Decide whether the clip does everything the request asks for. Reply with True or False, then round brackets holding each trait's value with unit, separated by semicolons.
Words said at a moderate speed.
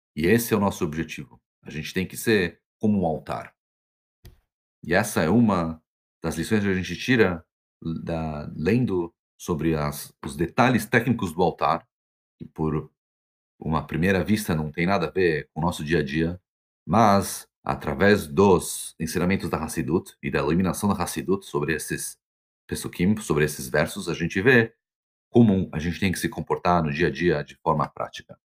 True (175 wpm)